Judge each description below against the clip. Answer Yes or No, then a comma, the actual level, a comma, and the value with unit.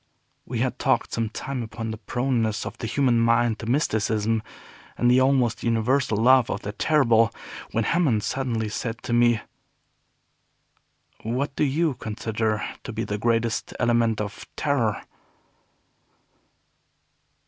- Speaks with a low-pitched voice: Yes, low, 115 Hz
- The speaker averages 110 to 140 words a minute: Yes, slow, 135 wpm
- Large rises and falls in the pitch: No, narrow, 2.6 semitones